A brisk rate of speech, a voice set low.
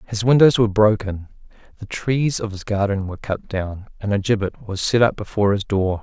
Yes: fast, 210 wpm; low, 105 Hz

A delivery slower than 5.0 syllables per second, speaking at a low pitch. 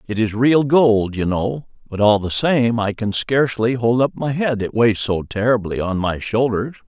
Yes: 4.5 syllables/s; low, 115 Hz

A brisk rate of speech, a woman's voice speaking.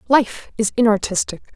No: slow, 115 wpm; female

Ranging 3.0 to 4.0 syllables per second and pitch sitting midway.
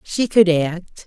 Yes: 3.1 syllables/s; medium, 180 Hz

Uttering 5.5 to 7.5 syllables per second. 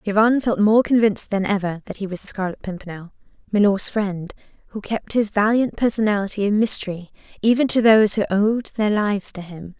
Yes: 5.8 syllables/s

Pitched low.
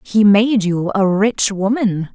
No: high, 205 Hz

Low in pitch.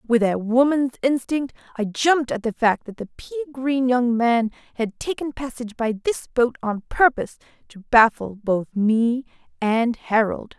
No: high, 240 Hz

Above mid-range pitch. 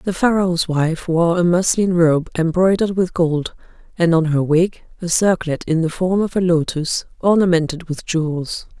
No: medium, 170 Hz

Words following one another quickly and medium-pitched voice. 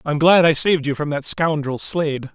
Yes: fast, 230 wpm; medium, 155 Hz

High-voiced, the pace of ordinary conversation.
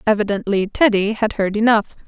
Yes: high, 210 Hz; average, 145 wpm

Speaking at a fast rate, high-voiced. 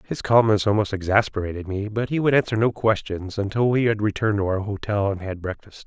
No: fast, 215 wpm; low, 105 Hz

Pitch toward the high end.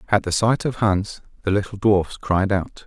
No: low, 100 Hz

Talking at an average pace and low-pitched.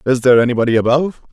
Yes: average, 180 wpm; low, 125 Hz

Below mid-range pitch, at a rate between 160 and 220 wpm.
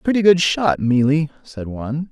No: medium, 155 Hz; average, 200 wpm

